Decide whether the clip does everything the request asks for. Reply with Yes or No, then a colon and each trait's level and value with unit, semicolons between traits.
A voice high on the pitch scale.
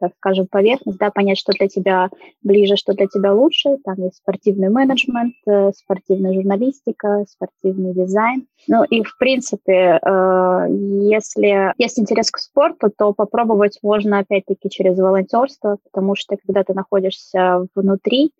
Yes: high, 200 Hz